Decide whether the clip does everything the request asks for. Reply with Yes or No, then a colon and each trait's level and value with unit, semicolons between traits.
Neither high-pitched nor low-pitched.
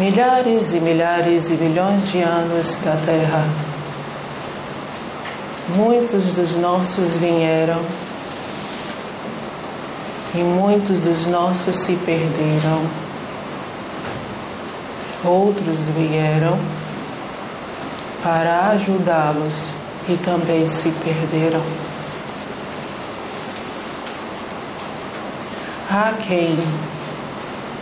Yes: medium, 170 Hz